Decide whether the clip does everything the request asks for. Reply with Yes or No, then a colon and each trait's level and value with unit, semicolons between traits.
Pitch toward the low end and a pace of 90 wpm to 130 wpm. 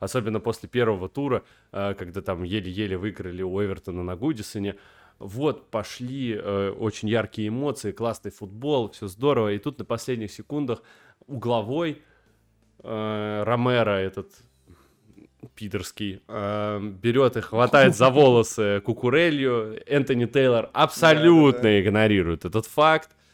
Yes: low, 110 Hz; slow, 110 wpm